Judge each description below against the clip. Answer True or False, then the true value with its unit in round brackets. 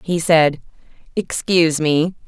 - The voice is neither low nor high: True (165 Hz)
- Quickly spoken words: False (105 wpm)